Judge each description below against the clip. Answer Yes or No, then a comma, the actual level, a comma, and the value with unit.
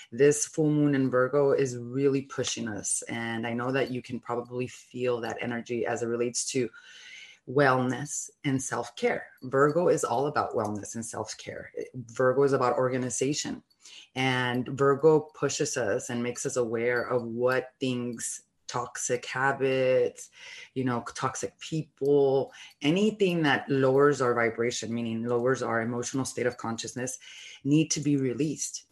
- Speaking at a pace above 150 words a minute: No, average, 145 wpm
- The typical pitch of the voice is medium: No, low, 130 Hz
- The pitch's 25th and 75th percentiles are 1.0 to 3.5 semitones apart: Yes, average, 2.7 semitones